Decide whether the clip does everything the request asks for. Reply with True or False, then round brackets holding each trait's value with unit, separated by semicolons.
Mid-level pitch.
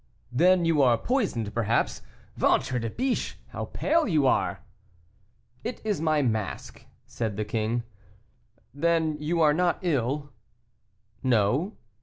True (145 Hz)